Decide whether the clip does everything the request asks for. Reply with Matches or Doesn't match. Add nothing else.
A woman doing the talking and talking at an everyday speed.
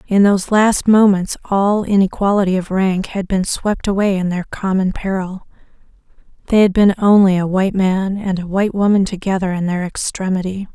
Matches